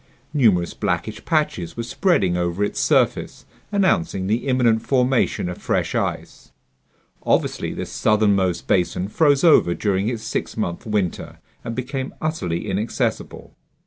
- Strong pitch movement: Yes, wide, 5.9 semitones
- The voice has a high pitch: No, low, 110 Hz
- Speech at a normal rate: No, slow, 130 wpm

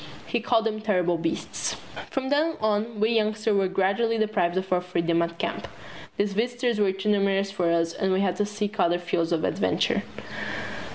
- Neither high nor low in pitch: No, high, 200 Hz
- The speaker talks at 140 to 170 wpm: No, average, 185 wpm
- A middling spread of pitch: Yes, average, 3.3 semitones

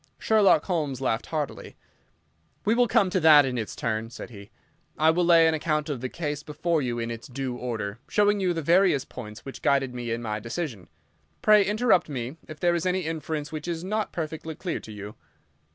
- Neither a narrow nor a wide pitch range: No, wide, 6.0 semitones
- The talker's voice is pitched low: No, medium, 150 Hz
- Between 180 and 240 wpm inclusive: Yes, fast, 205 wpm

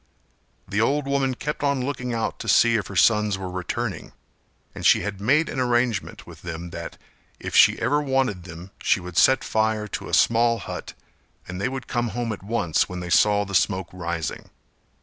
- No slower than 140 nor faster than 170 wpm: No, average, 195 wpm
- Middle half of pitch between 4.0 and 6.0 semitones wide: Yes, wide, 5.4 semitones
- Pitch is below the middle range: Yes, low, 110 Hz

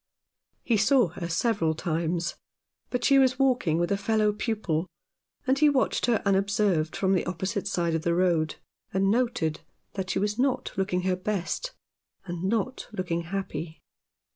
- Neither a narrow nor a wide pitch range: Yes, average, 4.6 semitones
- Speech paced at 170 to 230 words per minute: No, average, 160 wpm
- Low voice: No, high, 195 Hz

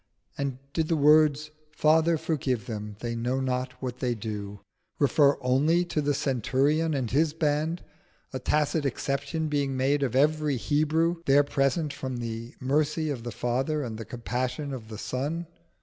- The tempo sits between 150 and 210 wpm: Yes, average, 165 wpm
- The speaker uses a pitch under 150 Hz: Yes, medium, 140 Hz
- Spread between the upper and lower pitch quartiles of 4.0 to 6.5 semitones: No, average, 3.4 semitones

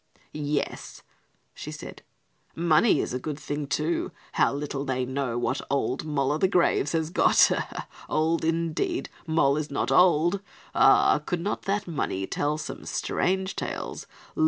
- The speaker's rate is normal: Yes, average, 150 wpm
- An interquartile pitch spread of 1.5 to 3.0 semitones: No, average, 3.4 semitones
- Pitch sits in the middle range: Yes, medium, 155 Hz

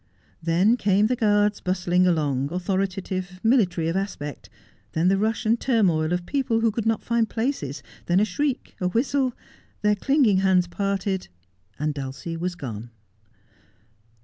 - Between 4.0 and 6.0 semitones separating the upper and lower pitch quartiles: Yes, average, 4.6 semitones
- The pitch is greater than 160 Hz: Yes, high, 190 Hz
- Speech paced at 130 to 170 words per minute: Yes, average, 160 wpm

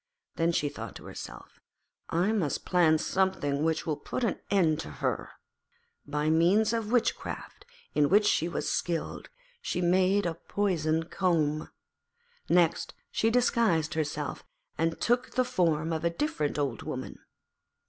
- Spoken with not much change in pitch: No, average, 4.2 semitones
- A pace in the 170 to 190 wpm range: No, average, 145 wpm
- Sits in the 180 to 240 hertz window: No, medium, 170 Hz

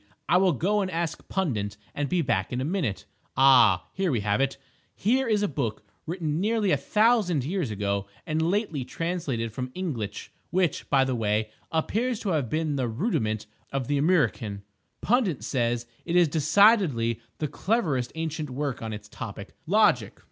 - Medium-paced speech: Yes, average, 170 wpm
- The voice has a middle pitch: Yes, medium, 150 Hz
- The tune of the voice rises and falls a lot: Yes, wide, 7.6 semitones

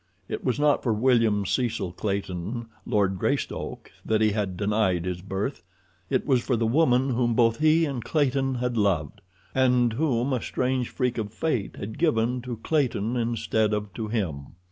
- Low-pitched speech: Yes, low, 115 Hz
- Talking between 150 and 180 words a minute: Yes, average, 170 wpm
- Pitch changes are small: No, average, 3.7 semitones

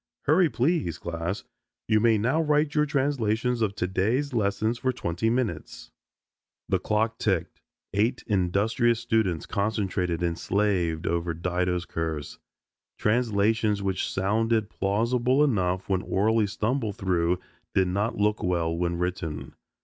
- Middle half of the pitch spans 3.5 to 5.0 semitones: Yes, average, 4.5 semitones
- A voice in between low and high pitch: No, low, 105 Hz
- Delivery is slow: Yes, slow, 125 wpm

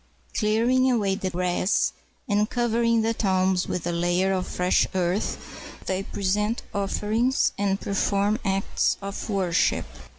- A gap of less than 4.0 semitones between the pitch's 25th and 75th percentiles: Yes, average, 2.9 semitones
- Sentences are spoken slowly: Yes, slow, 130 wpm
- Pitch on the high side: Yes, high, 200 Hz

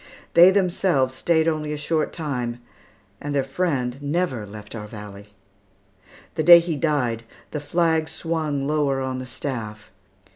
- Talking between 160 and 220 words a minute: No, average, 145 wpm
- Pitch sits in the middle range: Yes, medium, 145 Hz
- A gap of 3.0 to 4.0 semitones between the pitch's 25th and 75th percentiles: No, average, 4.7 semitones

